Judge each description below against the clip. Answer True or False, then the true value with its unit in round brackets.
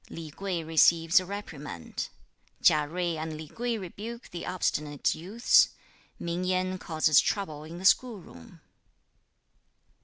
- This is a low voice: False (170 Hz)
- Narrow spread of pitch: False (3.3 semitones)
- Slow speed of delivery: True (130 wpm)